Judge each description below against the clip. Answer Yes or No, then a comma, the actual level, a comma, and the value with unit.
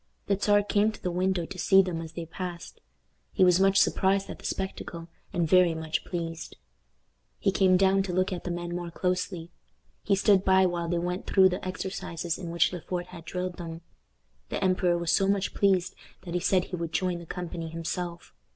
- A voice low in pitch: No, medium, 180 Hz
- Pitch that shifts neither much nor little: No, narrow, 1.8 semitones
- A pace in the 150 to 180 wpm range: No, fast, 205 wpm